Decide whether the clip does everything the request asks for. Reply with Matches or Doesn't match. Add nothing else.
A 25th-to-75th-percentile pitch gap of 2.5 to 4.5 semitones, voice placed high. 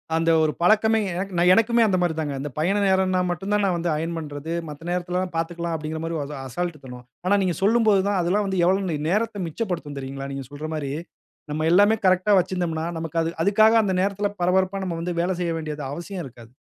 Doesn't match